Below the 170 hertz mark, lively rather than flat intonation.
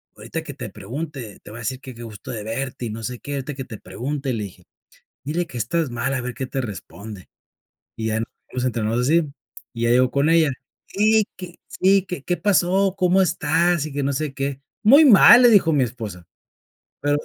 Yes: low, 135 Hz; wide, 6.2 semitones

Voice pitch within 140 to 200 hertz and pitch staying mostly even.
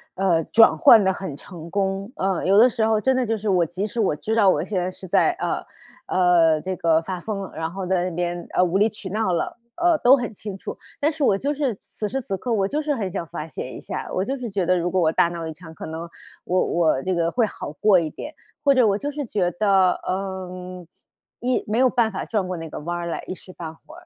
No: high, 190 Hz; average, 4.3 semitones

